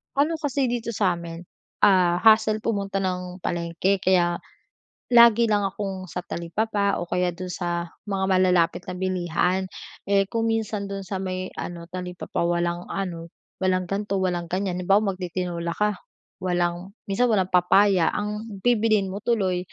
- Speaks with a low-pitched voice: No, medium, 185 Hz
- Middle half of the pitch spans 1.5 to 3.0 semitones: Yes, narrow, 2.6 semitones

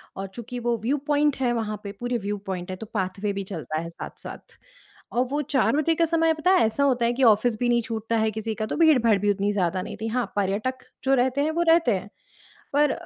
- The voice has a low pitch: No, high, 230 Hz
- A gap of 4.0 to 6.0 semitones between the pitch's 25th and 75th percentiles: Yes, average, 4.6 semitones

